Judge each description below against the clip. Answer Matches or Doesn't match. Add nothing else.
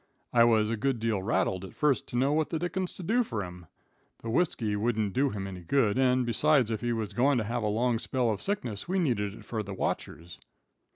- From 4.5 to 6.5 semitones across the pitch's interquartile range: Matches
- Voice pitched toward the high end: Doesn't match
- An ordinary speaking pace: Doesn't match